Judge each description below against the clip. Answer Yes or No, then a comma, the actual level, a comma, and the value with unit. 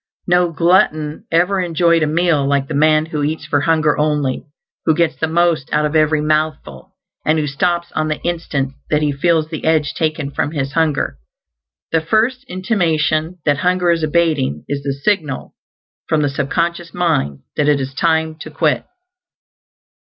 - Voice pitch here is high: No, medium, 155 Hz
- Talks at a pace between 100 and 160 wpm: No, average, 175 wpm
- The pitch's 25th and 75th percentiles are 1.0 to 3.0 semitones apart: Yes, narrow, 2.5 semitones